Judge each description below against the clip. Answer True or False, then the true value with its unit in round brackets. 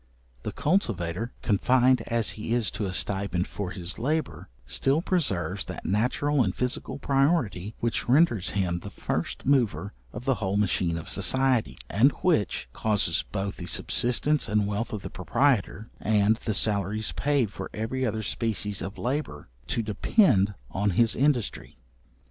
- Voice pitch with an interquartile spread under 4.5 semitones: False (4.8 semitones)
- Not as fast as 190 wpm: True (155 wpm)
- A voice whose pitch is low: True (110 Hz)